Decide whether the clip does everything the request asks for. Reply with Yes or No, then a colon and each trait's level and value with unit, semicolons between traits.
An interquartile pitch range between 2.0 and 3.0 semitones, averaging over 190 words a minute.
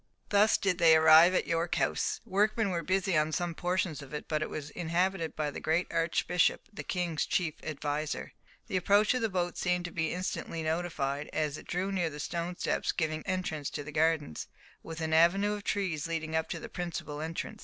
Yes: average, 2.7 semitones; fast, 205 wpm